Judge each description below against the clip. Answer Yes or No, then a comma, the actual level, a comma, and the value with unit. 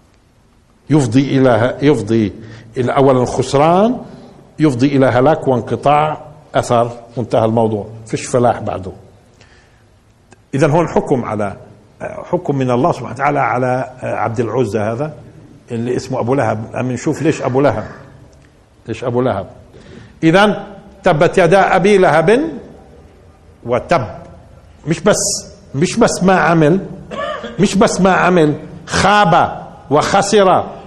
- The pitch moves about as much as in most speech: No, wide, 6.6 semitones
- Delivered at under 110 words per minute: No, average, 115 wpm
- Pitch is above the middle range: No, low, 135 Hz